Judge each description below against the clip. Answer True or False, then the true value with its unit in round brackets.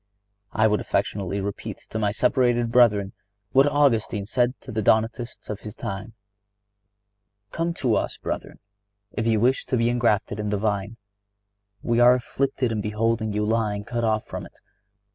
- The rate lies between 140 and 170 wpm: True (160 wpm)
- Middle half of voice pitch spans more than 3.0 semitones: False (2.5 semitones)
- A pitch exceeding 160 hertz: False (110 Hz)